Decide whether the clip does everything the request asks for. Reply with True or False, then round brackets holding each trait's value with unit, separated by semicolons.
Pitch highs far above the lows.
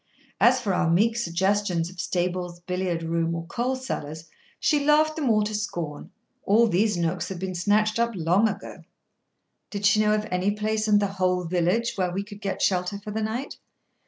False (3.5 semitones)